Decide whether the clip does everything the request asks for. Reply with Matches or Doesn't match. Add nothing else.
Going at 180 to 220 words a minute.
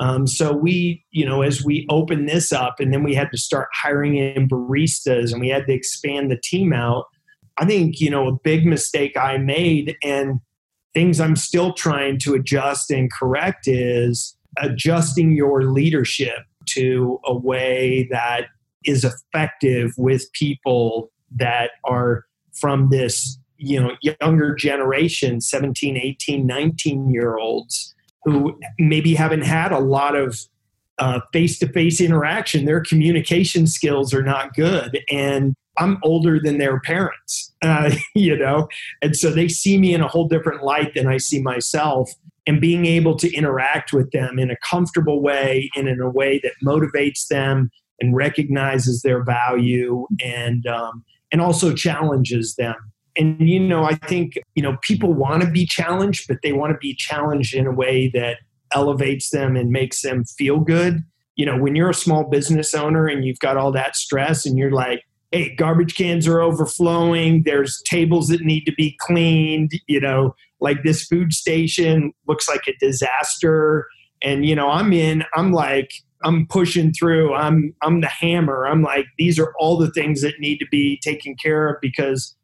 Doesn't match